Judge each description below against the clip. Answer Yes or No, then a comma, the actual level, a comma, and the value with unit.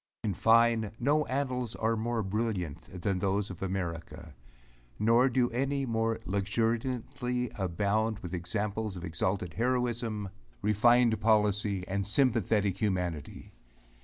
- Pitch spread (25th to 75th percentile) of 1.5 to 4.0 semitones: Yes, average, 3.5 semitones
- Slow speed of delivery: Yes, slow, 115 wpm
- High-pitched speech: No, low, 110 Hz